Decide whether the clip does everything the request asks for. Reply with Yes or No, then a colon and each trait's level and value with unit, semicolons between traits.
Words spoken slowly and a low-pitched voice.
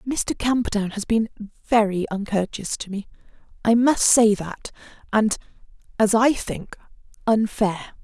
No: slow, 120 wpm; high, 215 Hz